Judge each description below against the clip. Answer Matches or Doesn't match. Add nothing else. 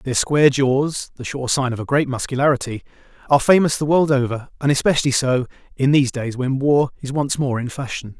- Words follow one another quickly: Doesn't match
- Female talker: Doesn't match